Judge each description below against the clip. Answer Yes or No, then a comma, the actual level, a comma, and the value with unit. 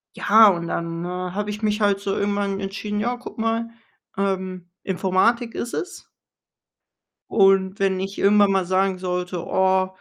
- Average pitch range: No, narrow, 1.9 semitones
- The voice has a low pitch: No, high, 195 Hz